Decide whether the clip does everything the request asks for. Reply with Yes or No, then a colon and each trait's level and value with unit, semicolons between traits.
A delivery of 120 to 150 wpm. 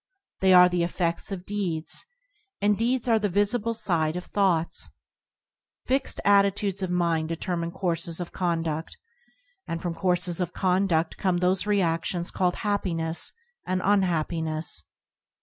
Yes: average, 140 wpm